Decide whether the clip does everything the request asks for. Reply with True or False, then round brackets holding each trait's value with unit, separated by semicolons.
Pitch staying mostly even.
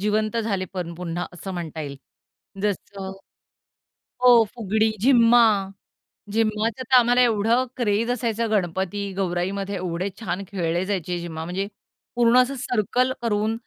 False (4.3 semitones)